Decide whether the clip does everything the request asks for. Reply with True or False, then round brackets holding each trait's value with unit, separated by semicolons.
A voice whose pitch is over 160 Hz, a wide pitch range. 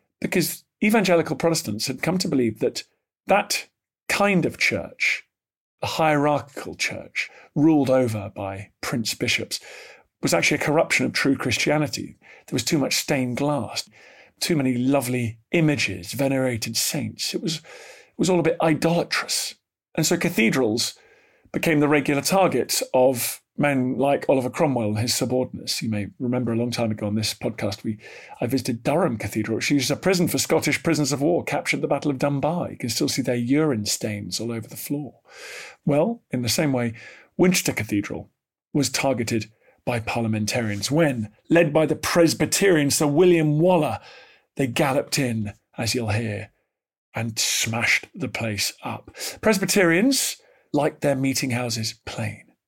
False (135 Hz; 5.7 semitones)